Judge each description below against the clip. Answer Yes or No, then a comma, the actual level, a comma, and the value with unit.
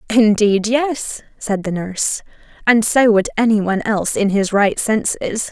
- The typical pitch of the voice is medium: No, high, 215 Hz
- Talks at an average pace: Yes, average, 165 wpm